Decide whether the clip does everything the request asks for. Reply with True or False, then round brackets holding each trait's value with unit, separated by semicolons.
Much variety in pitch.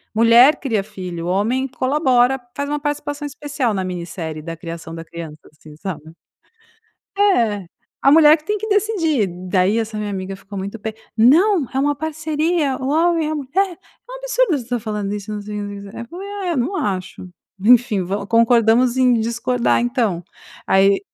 True (6.9 semitones)